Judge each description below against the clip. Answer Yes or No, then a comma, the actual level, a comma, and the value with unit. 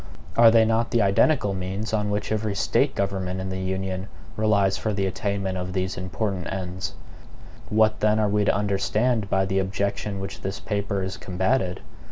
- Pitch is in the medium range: No, low, 100 Hz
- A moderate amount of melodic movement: No, narrow, 2.1 semitones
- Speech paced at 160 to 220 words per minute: Yes, average, 180 wpm